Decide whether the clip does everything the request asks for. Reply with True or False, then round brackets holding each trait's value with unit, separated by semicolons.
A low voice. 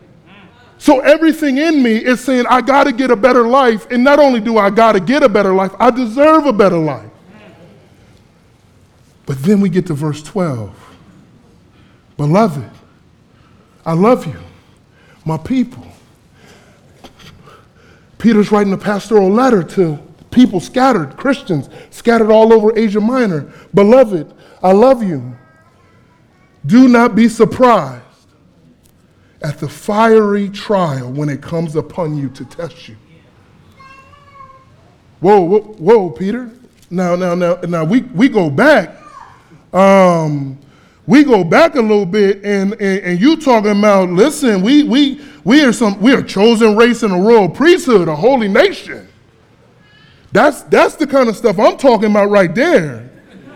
False (210 Hz)